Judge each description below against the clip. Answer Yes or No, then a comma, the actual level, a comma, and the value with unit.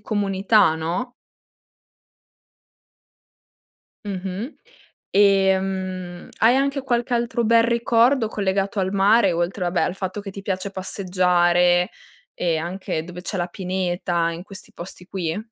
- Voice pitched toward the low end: No, high, 190 Hz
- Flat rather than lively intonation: No, average, 3.0 semitones